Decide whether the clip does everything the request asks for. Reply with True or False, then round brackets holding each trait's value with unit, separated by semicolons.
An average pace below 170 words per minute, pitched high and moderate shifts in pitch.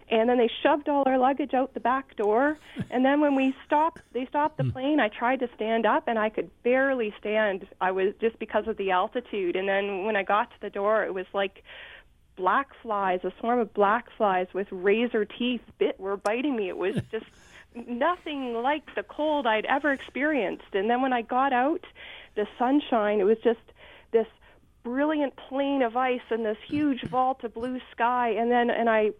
False (205 wpm; 240 Hz; 4.1 semitones)